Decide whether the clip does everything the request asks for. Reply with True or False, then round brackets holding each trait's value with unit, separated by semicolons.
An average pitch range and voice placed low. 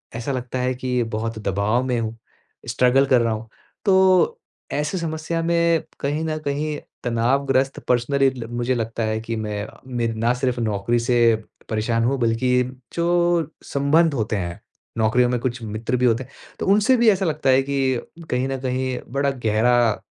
True (3.6 semitones; 125 Hz)